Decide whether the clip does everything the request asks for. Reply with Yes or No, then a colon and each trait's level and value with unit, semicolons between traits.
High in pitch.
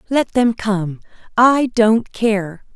Yes: high, 220 Hz